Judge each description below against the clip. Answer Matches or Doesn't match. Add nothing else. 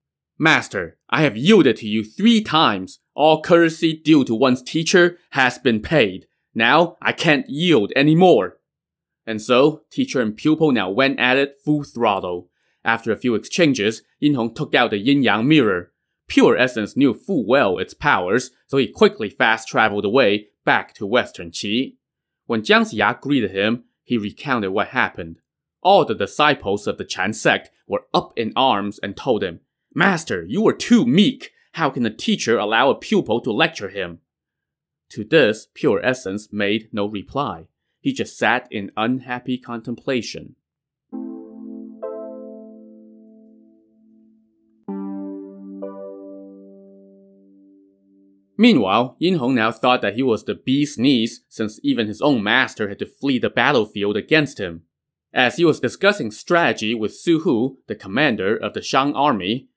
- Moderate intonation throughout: Doesn't match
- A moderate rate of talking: Matches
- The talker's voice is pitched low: Matches